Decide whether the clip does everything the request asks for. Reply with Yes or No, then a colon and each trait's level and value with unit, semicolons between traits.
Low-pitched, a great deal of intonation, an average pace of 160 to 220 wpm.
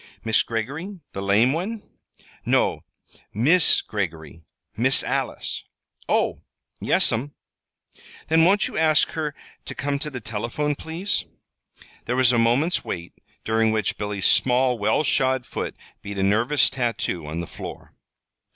No: low, 120 Hz; wide, 6.1 semitones; slow, 135 wpm